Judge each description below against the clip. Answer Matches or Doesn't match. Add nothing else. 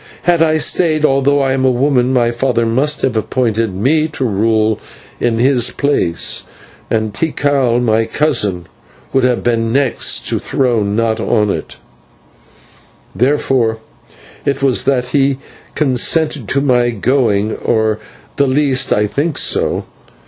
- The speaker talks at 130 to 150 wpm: Matches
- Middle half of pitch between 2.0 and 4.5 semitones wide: Matches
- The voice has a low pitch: Matches